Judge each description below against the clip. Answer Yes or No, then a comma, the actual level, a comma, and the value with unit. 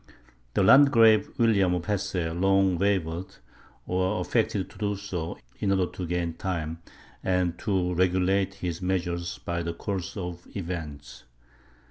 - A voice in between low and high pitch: No, very low, 90 Hz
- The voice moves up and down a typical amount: No, narrow, 2.2 semitones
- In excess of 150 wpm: No, slow, 135 wpm